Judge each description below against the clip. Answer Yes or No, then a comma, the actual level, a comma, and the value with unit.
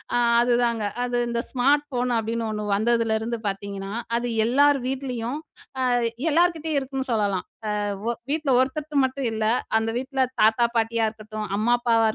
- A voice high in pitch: Yes, high, 240 Hz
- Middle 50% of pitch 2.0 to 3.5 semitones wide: Yes, average, 3.2 semitones